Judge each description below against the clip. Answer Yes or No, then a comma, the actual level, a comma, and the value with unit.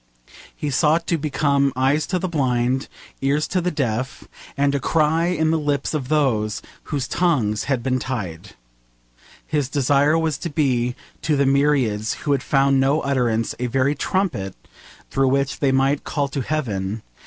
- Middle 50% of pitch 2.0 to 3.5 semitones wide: Yes, average, 3.0 semitones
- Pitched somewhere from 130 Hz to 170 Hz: Yes, medium, 140 Hz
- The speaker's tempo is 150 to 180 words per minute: Yes, average, 165 wpm